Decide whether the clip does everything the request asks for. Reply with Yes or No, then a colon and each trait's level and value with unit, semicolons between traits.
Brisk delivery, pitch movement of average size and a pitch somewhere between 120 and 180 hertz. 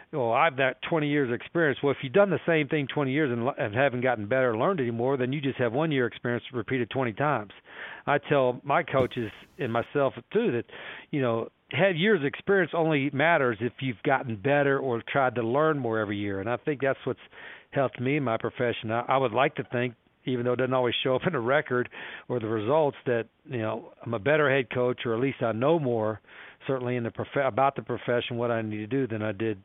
Yes: fast, 245 wpm; average, 3.2 semitones; low, 130 Hz